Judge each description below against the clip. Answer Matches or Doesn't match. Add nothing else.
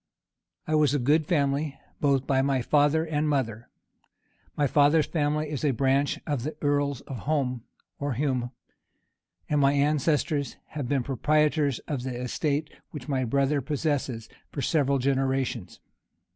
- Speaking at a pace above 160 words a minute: Doesn't match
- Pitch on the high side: Doesn't match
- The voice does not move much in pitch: Matches